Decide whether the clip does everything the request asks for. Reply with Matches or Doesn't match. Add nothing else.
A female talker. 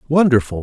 Doesn't match